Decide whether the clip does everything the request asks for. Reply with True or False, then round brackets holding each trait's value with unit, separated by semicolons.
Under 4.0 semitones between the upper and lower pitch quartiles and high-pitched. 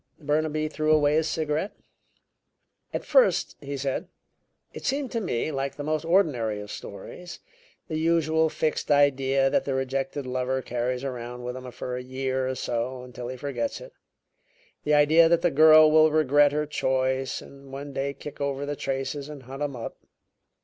False (2.9 semitones; 140 Hz)